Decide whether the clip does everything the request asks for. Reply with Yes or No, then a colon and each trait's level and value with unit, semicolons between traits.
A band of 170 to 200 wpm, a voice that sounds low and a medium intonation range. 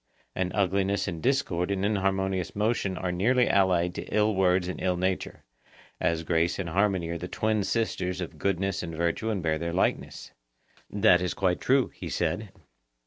No: average, 175 wpm; very low, 95 Hz; narrow, 2.3 semitones